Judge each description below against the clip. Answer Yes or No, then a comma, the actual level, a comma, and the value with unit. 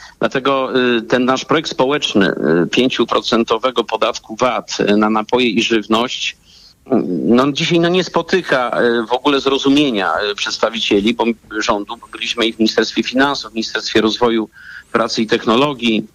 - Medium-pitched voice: No, low, 120 Hz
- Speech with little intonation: No, average, 3.6 semitones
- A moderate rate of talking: Yes, average, 125 wpm